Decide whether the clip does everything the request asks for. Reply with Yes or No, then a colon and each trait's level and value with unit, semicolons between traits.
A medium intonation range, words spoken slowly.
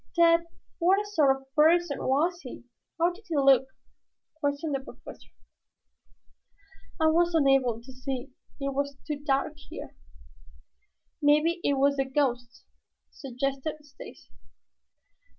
Yes: average, 3.5 semitones; slow, 120 wpm